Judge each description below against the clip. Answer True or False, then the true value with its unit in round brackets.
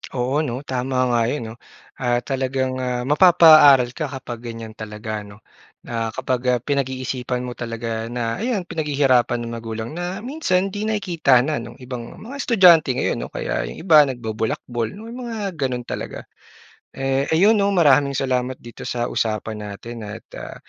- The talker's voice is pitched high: False (130 Hz)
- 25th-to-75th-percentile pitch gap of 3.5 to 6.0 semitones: True (5.0 semitones)